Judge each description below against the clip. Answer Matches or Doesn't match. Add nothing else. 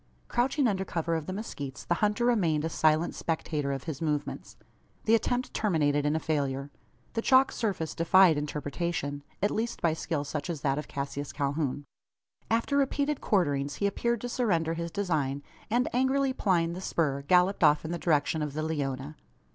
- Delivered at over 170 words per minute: Matches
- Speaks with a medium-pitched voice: Matches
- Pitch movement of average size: Doesn't match